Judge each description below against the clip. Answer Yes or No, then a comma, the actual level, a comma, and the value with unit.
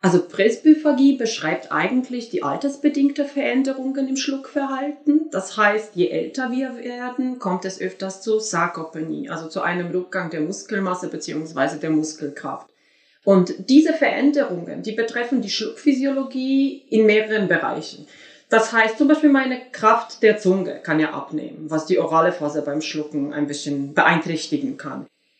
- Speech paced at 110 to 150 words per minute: Yes, average, 140 wpm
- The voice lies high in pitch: Yes, high, 215 Hz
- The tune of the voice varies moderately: No, wide, 8.2 semitones